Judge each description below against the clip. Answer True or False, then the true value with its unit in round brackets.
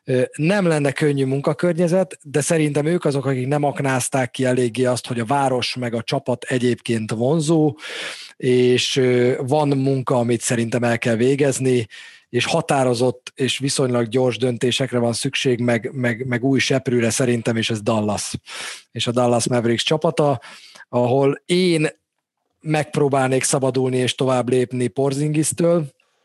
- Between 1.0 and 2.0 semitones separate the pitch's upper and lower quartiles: False (2.9 semitones)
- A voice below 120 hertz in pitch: False (130 Hz)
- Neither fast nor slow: True (135 wpm)